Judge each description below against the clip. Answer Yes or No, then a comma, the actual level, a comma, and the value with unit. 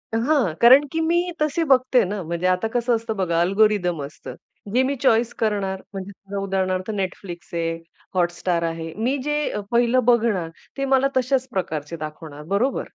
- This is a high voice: Yes, high, 205 Hz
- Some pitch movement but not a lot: No, wide, 6.1 semitones